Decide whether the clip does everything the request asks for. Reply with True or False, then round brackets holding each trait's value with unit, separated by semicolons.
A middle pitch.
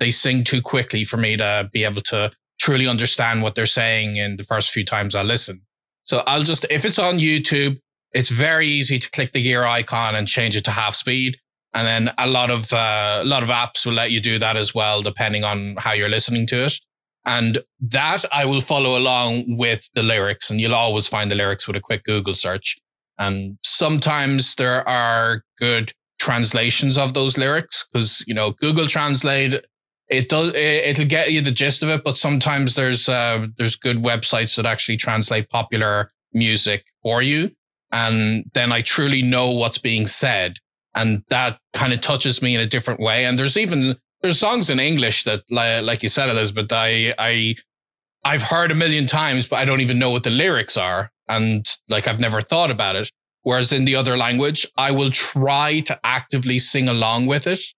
False (120 Hz)